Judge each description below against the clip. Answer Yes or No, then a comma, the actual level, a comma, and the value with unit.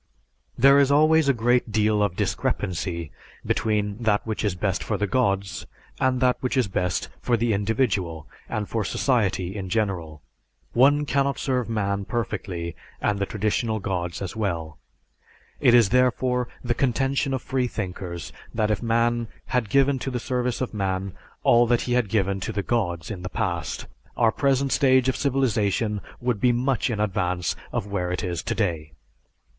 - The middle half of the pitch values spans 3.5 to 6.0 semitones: Yes, average, 4.5 semitones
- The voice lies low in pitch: Yes, low, 110 Hz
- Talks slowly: No, average, 170 wpm